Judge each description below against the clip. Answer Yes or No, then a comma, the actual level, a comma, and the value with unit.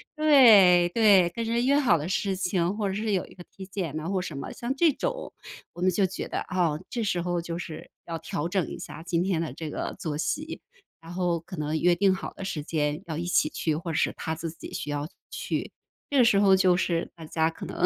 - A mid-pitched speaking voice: Yes, medium, 180 Hz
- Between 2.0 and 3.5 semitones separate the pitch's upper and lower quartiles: Yes, average, 3.2 semitones